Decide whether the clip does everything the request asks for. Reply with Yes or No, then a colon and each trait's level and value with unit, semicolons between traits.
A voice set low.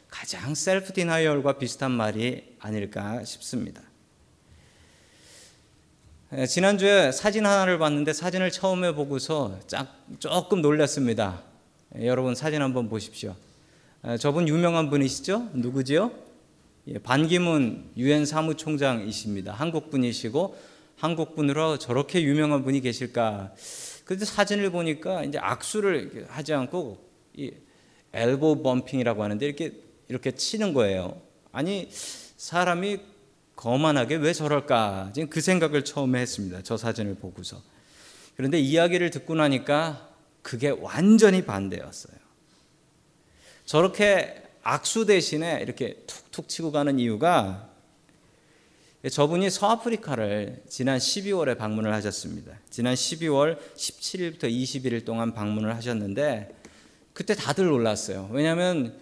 No: medium, 145 Hz